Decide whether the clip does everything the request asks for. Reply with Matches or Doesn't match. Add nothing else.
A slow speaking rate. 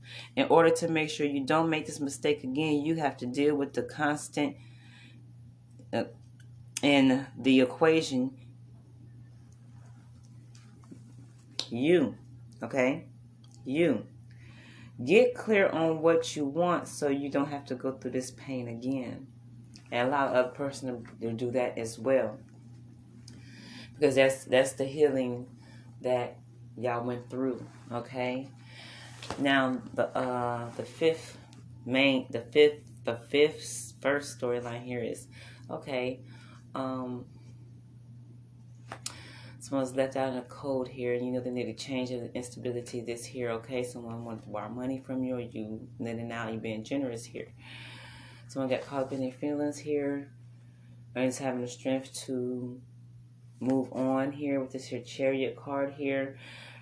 Doesn't match